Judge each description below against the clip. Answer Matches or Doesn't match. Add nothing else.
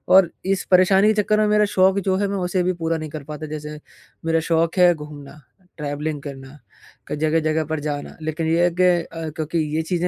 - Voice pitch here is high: Doesn't match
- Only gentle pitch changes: Doesn't match